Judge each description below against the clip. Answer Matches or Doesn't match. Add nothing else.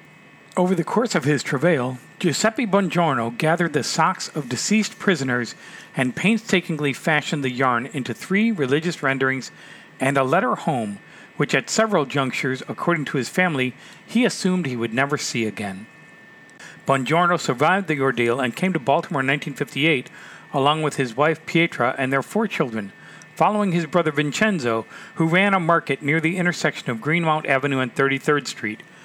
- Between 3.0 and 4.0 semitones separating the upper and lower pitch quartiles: Doesn't match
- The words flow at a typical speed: Matches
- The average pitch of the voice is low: Doesn't match